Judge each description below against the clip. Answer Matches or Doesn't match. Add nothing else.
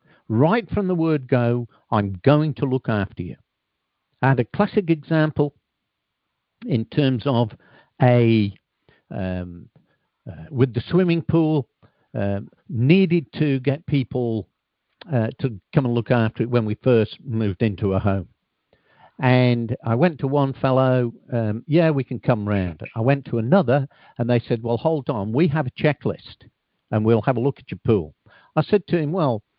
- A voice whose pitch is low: Matches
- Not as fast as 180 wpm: Matches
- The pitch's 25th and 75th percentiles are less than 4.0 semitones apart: Doesn't match